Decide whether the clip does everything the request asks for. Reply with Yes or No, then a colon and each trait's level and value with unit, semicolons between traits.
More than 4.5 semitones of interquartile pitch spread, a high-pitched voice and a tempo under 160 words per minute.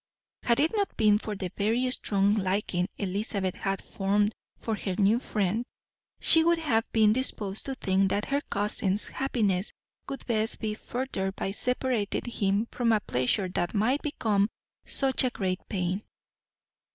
No: average, 3.7 semitones; high, 210 Hz; average, 150 wpm